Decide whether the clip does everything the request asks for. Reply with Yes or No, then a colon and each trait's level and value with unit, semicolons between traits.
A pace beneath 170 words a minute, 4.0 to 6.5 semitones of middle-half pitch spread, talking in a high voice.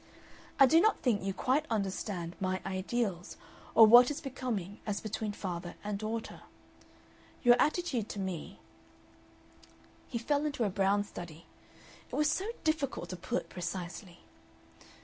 Yes: average, 145 wpm; wide, 5.4 semitones; high, 210 Hz